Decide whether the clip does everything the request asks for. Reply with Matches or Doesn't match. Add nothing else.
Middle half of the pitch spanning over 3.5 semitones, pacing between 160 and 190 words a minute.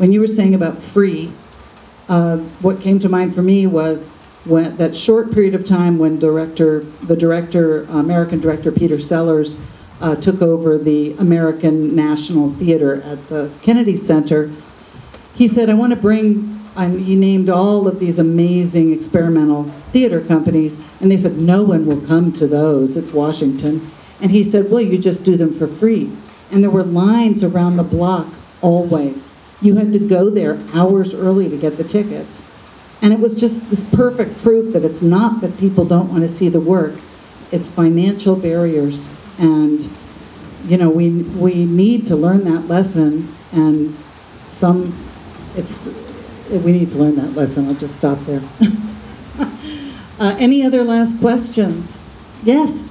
Matches